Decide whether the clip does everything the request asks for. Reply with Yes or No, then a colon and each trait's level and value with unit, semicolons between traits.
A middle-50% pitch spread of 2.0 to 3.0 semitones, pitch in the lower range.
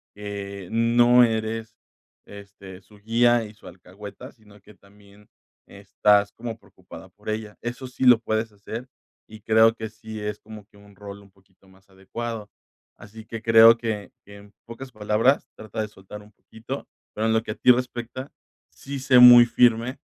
Yes: narrow, 2.4 semitones; low, 110 Hz